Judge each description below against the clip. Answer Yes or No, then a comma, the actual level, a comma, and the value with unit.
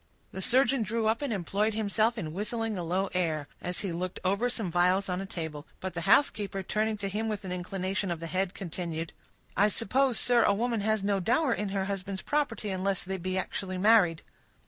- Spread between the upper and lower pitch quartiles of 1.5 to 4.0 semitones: Yes, average, 3.2 semitones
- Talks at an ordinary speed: No, fast, 210 wpm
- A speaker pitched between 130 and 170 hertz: No, high, 195 Hz